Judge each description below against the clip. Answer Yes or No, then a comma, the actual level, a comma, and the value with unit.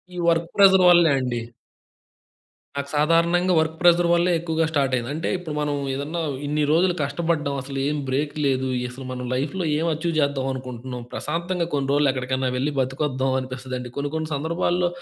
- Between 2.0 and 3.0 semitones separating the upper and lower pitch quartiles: No, average, 4.2 semitones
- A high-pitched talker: No, medium, 150 Hz